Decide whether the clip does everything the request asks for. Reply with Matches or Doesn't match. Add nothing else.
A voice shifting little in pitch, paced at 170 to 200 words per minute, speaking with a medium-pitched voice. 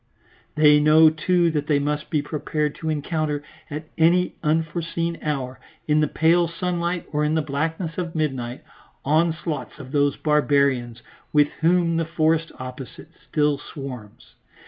Doesn't match